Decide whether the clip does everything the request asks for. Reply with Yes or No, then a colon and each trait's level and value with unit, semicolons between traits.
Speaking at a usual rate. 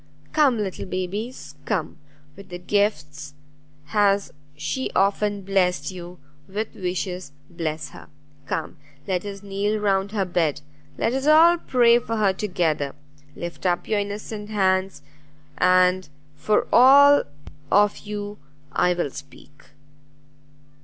No: slow, 120 wpm